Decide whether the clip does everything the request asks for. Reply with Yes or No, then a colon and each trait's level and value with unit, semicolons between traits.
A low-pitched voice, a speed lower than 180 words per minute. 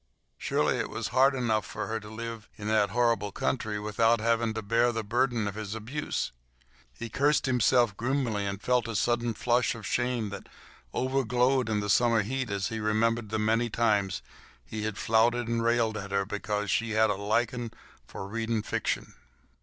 No: low, 115 Hz; average, 185 wpm